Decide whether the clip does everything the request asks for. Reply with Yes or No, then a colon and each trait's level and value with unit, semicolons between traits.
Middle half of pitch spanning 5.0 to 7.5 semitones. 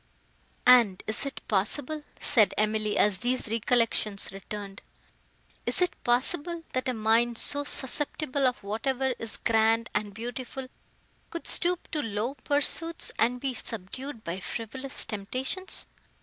No: average, 4.1 semitones